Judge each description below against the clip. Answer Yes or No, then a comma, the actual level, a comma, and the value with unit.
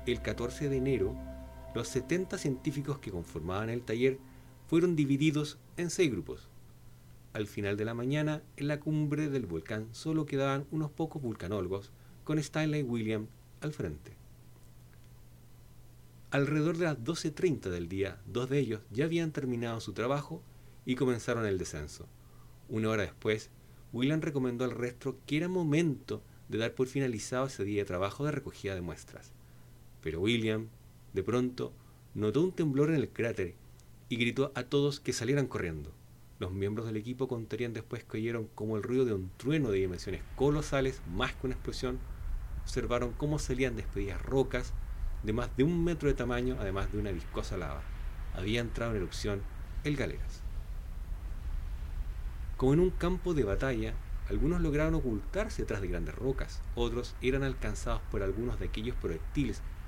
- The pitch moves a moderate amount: No, wide, 6.0 semitones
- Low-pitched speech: Yes, low, 120 Hz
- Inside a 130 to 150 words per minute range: No, average, 160 wpm